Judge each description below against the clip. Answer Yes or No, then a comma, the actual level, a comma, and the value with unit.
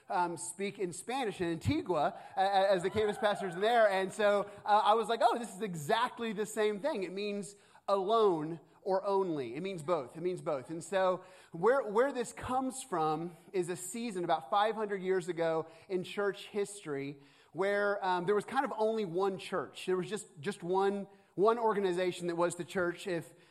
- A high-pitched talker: Yes, high, 195 Hz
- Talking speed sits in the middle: No, fast, 190 wpm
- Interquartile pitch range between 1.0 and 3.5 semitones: Yes, average, 2.9 semitones